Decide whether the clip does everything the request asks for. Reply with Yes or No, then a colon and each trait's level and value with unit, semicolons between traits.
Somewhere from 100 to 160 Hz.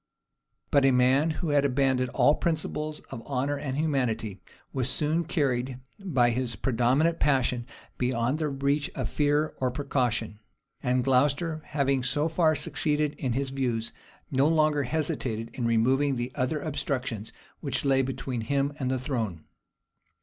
Yes: low, 135 Hz